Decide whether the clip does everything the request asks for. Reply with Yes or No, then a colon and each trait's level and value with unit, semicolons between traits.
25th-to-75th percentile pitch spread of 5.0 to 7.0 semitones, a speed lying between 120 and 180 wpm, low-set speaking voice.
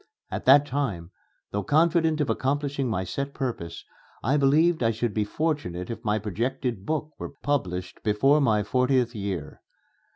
Yes: wide, 5.5 semitones; average, 155 wpm; low, 125 Hz